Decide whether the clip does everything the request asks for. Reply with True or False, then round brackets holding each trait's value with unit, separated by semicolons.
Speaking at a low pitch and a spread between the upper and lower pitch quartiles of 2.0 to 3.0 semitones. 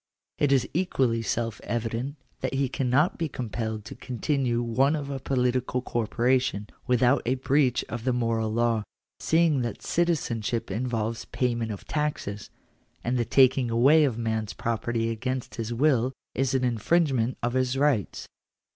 True (125 Hz; 2.7 semitones)